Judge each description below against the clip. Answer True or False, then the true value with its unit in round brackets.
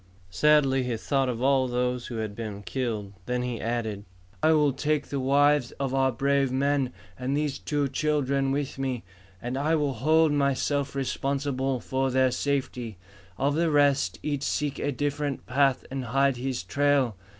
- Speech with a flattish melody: True (2.3 semitones)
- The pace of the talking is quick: False (165 wpm)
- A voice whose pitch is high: False (135 Hz)